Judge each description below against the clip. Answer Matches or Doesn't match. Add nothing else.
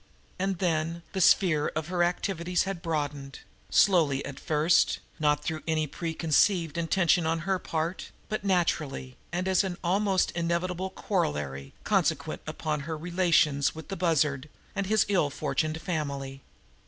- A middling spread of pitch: Matches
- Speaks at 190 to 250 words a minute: Doesn't match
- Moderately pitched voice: Matches